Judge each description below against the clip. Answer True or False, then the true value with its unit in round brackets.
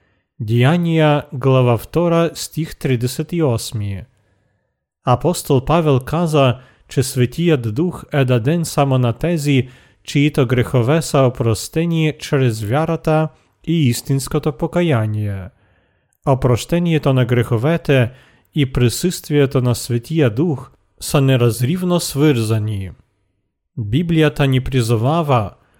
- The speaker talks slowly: True (100 wpm)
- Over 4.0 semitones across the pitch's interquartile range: True (4.6 semitones)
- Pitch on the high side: False (135 Hz)